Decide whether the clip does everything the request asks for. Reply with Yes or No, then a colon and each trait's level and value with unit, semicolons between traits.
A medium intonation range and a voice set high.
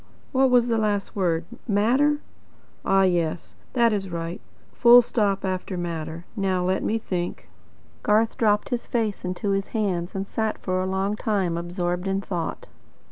Yes: average, 3.5 semitones; high, 195 Hz